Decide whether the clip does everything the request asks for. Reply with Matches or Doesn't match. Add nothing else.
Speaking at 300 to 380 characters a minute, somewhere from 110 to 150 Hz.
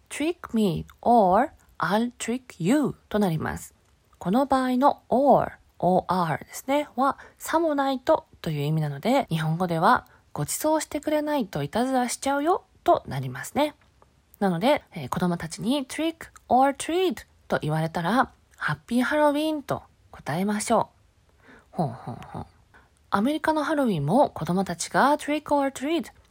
Doesn't match